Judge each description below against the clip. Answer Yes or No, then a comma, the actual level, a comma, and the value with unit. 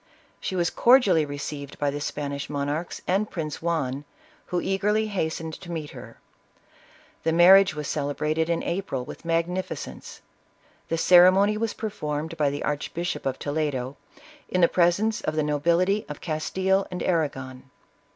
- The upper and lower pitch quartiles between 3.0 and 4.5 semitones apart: Yes, average, 4.0 semitones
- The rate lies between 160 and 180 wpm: No, average, 150 wpm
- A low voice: No, medium, 165 Hz